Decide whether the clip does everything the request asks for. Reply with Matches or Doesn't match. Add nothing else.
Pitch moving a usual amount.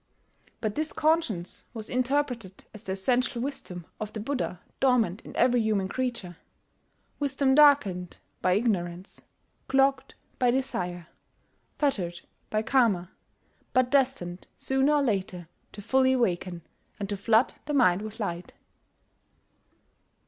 Doesn't match